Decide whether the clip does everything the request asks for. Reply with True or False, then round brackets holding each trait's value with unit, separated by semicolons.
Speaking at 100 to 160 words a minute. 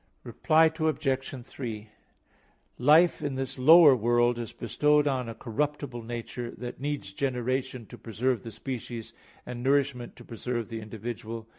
True (140 wpm)